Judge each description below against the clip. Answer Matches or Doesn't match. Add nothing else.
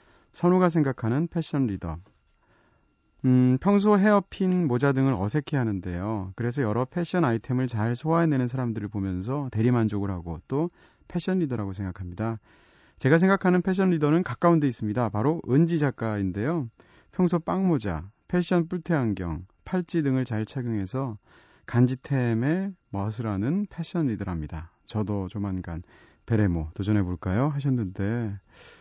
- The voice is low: Matches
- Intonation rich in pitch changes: Matches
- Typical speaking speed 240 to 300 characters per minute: Doesn't match